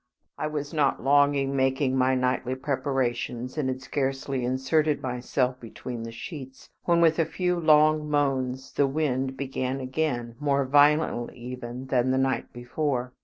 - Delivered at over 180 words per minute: No, average, 155 wpm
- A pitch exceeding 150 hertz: No, low, 135 Hz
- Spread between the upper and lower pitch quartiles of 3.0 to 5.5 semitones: No, narrow, 2.4 semitones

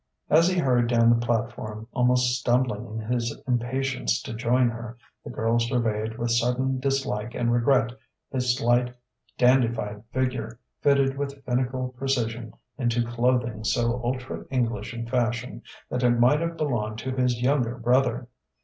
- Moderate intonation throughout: No, narrow, 1.7 semitones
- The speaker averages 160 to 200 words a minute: No, average, 150 wpm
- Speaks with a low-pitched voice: Yes, low, 120 Hz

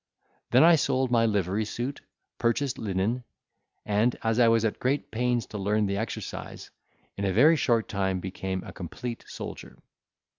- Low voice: Yes, low, 115 Hz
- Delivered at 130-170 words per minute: Yes, average, 160 wpm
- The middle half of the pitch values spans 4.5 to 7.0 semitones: No, average, 3.8 semitones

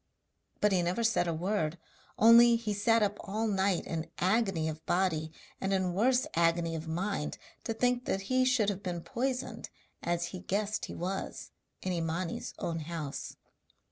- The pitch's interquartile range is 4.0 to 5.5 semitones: Yes, average, 4.5 semitones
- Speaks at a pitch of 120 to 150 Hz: No, high, 190 Hz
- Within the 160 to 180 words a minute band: Yes, average, 170 wpm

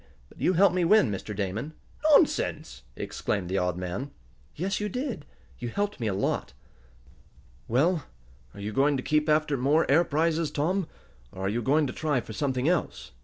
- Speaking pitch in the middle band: Yes, medium, 145 Hz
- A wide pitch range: Yes, wide, 7.4 semitones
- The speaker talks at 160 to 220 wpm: Yes, average, 180 wpm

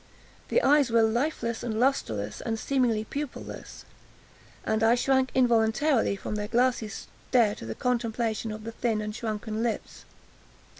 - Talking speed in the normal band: Yes, average, 145 wpm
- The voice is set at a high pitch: Yes, high, 230 Hz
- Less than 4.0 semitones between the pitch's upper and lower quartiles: Yes, narrow, 2.5 semitones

